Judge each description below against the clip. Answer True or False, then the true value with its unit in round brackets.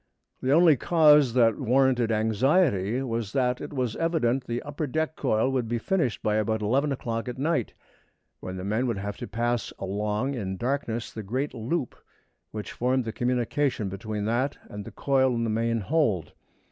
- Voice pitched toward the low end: True (120 Hz)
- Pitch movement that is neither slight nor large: True (3.8 semitones)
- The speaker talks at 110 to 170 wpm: False (180 wpm)